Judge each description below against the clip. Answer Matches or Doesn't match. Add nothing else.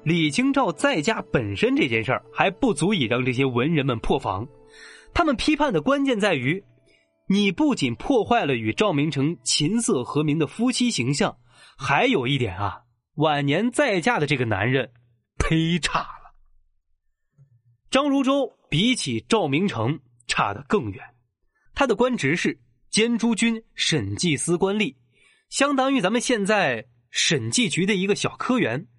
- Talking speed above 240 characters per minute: Doesn't match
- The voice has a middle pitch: Matches